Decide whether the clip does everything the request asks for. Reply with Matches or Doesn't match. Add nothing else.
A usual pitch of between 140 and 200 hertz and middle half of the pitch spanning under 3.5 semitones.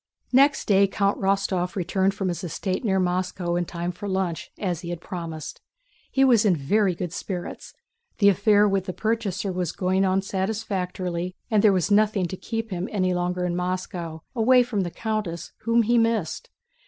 Matches